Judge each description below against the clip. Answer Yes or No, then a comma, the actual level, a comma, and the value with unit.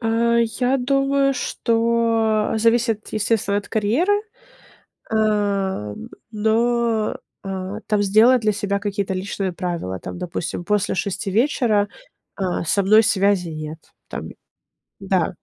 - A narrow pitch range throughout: No, average, 3.0 semitones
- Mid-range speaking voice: No, high, 210 Hz